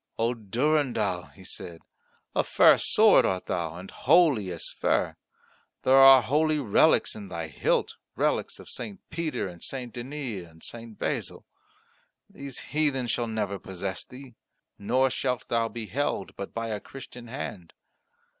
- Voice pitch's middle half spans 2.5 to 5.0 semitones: No, wide, 5.6 semitones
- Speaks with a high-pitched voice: No, low, 115 Hz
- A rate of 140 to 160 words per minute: Yes, average, 150 wpm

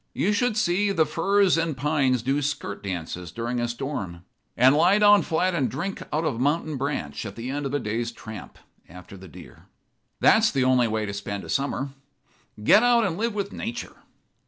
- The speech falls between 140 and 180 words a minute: No, average, 200 wpm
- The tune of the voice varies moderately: No, wide, 8.2 semitones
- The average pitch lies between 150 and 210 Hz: No, medium, 140 Hz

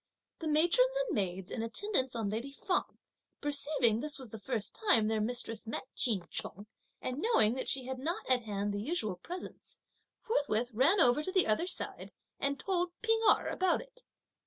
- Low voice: No, very high, 260 Hz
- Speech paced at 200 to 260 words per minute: No, average, 185 wpm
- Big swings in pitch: Yes, wide, 7.8 semitones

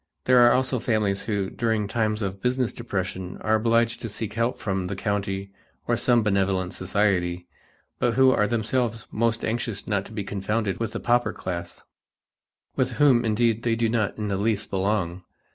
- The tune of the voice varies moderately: Yes, average, 3.1 semitones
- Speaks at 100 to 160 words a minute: No, average, 180 wpm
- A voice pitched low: Yes, low, 110 Hz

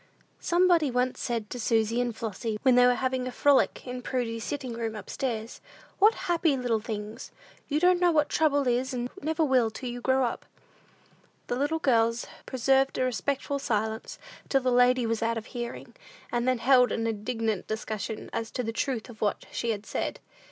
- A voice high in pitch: Yes, high, 245 Hz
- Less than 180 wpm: No, average, 190 wpm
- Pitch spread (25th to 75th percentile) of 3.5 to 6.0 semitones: No, average, 2.9 semitones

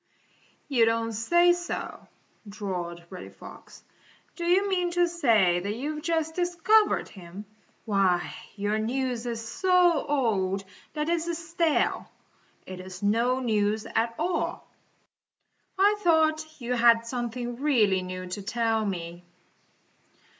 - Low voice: No, high, 235 Hz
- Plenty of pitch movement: Yes, wide, 8.1 semitones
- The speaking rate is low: Yes, slow, 125 wpm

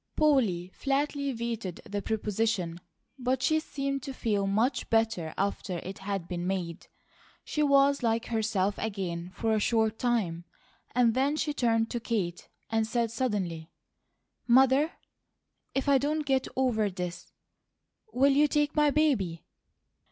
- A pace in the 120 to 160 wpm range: Yes, average, 140 wpm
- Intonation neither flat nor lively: No, wide, 5.7 semitones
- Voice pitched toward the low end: No, high, 225 Hz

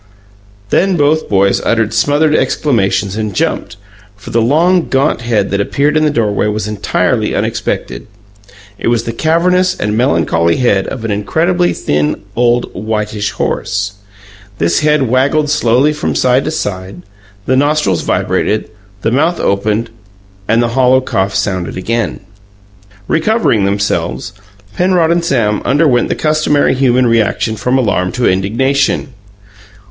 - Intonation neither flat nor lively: No, wide, 6.3 semitones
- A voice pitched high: No, low, 120 Hz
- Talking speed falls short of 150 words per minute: Yes, average, 140 wpm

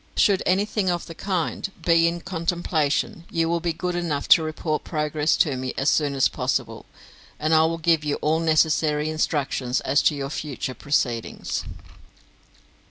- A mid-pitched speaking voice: Yes, medium, 155 Hz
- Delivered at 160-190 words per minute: Yes, average, 165 wpm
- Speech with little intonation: Yes, narrow, 2.3 semitones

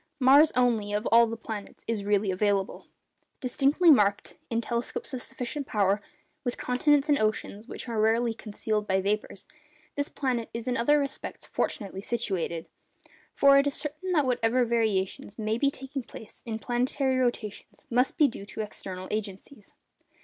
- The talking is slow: No, average, 160 wpm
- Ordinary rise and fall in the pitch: Yes, average, 4.0 semitones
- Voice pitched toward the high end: Yes, high, 230 Hz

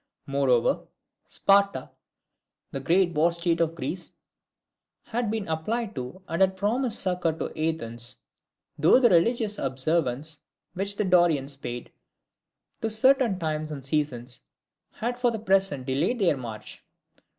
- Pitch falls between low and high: Yes, medium, 170 Hz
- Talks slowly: Yes, slow, 130 wpm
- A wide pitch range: Yes, wide, 6.3 semitones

